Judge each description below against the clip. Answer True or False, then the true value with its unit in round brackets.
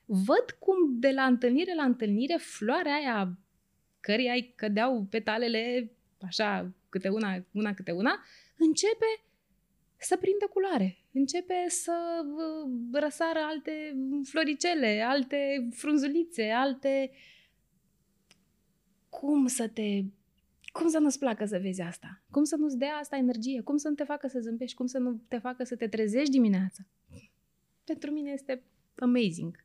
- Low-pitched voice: False (260 Hz)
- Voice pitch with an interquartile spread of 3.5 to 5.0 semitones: False (5.4 semitones)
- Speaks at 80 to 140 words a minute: True (135 wpm)